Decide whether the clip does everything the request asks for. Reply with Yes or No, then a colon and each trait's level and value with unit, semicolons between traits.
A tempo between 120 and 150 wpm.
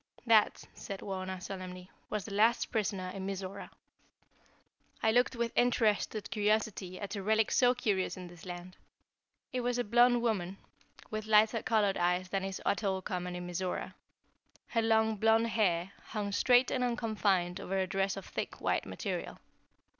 No: average, 160 wpm